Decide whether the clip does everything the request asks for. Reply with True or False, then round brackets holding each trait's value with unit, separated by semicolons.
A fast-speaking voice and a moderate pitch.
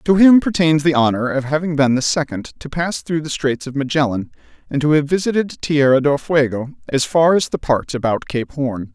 True (215 wpm; 145 Hz)